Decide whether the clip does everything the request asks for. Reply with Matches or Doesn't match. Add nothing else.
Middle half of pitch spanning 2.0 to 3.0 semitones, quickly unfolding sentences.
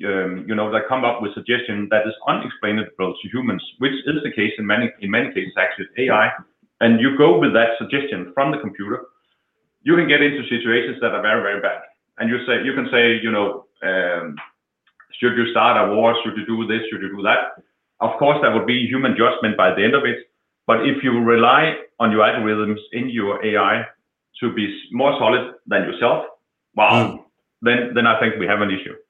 Matches